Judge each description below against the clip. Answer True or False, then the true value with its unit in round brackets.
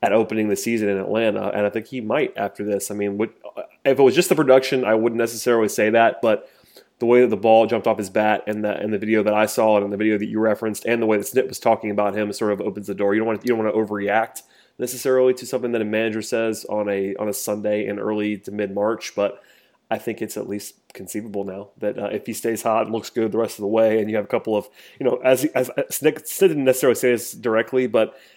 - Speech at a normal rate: False (280 wpm)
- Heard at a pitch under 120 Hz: True (110 Hz)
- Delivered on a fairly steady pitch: True (2.0 semitones)